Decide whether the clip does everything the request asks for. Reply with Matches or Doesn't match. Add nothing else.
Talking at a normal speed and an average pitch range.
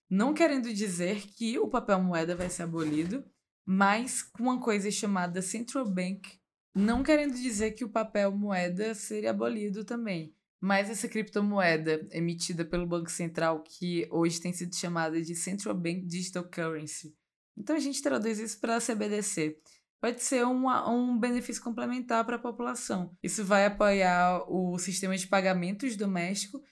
Matches